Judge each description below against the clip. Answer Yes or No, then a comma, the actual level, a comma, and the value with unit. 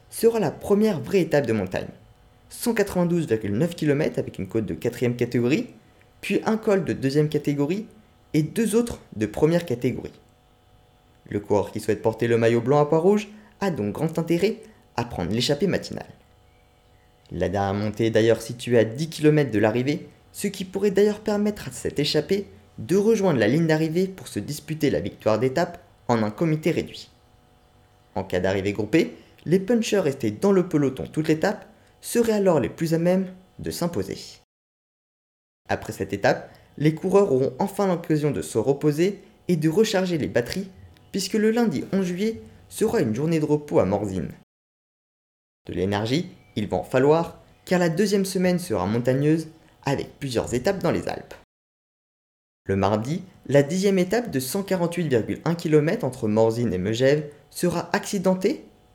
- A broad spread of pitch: Yes, wide, 7.8 semitones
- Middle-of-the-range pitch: Yes, medium, 150 Hz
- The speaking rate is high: No, average, 165 wpm